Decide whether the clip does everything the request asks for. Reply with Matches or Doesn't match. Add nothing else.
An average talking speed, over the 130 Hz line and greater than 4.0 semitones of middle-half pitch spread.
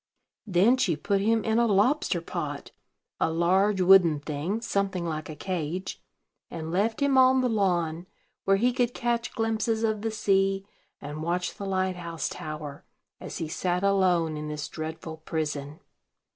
Matches